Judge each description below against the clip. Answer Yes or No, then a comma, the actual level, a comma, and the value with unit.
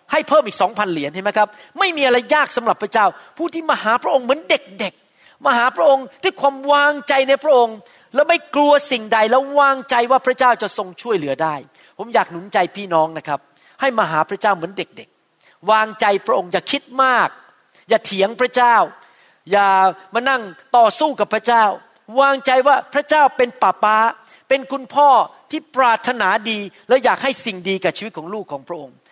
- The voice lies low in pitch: No, high, 235 Hz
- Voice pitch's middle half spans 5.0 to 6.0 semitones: Yes, wide, 5.6 semitones